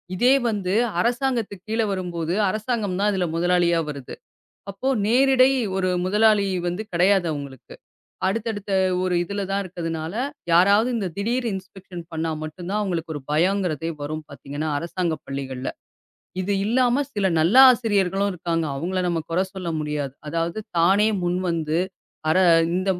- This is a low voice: No, medium, 185 Hz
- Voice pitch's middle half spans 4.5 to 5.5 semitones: No, average, 3.7 semitones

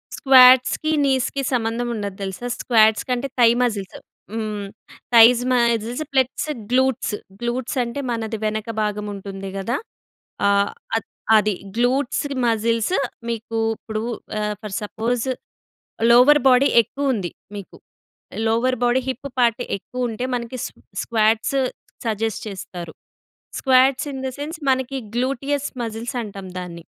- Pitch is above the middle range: Yes, high, 235 Hz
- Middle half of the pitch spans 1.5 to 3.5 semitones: Yes, average, 3.2 semitones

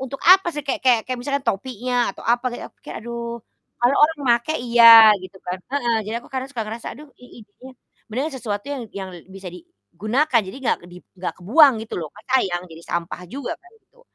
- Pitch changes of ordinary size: Yes, average, 4.7 semitones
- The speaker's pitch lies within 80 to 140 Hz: No, high, 235 Hz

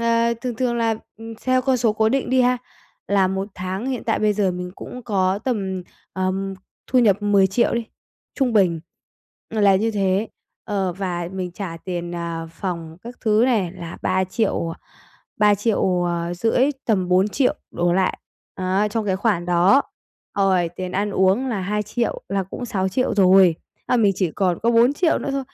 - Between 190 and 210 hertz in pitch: Yes, high, 195 Hz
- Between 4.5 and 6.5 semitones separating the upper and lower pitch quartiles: No, average, 3.8 semitones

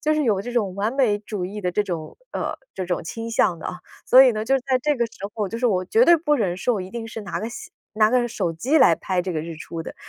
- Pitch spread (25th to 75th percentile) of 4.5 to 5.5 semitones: Yes, average, 5.1 semitones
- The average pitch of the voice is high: Yes, high, 215 Hz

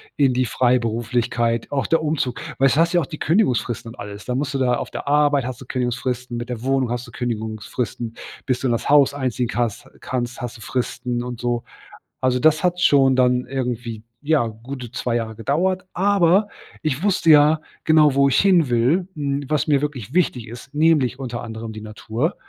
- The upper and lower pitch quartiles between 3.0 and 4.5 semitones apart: Yes, average, 3.6 semitones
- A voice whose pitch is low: Yes, low, 125 Hz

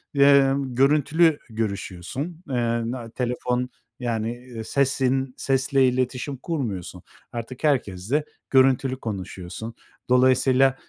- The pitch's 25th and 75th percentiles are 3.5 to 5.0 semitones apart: No, average, 2.7 semitones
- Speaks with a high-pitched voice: No, low, 125 Hz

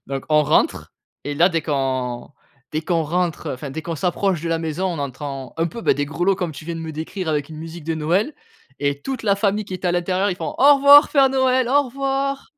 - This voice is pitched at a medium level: Yes, medium, 170 Hz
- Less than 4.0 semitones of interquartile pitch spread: No, average, 5.0 semitones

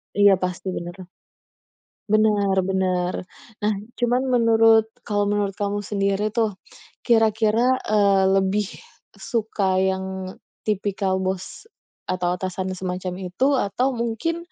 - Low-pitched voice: No, high, 200 Hz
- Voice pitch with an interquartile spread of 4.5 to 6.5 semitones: No, average, 2.8 semitones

